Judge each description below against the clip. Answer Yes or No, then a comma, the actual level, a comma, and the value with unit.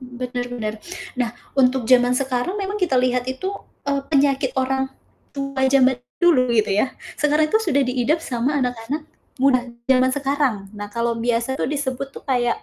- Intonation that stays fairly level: Yes, narrow, 2.3 semitones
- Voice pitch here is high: Yes, very high, 260 Hz